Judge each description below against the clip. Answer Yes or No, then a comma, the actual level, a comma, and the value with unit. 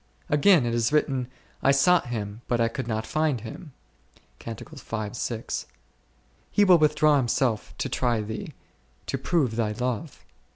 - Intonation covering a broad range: No, average, 4.8 semitones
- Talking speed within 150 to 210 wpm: No, average, 140 wpm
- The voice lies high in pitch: No, low, 125 Hz